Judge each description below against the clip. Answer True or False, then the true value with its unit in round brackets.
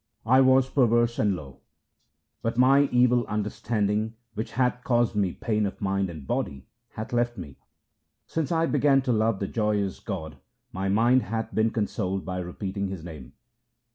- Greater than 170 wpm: False (165 wpm)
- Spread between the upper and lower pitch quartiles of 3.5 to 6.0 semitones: True (4.1 semitones)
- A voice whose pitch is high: False (110 Hz)